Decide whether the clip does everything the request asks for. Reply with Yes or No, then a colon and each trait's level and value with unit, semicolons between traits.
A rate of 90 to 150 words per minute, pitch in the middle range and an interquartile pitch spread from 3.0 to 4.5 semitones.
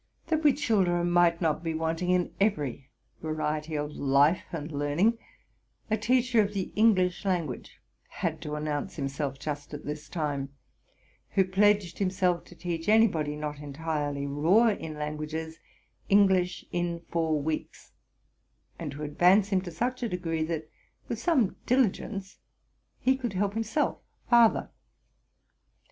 No: average, 140 wpm; medium, 170 Hz; average, 5.0 semitones